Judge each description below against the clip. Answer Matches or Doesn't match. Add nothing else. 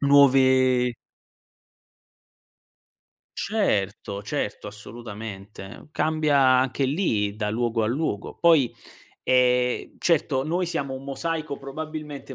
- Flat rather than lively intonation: Doesn't match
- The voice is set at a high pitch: Doesn't match